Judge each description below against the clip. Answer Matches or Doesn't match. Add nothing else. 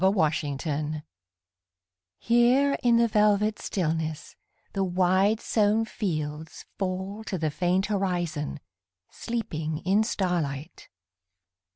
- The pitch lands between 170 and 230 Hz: Matches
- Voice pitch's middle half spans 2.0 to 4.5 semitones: Doesn't match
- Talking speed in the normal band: Doesn't match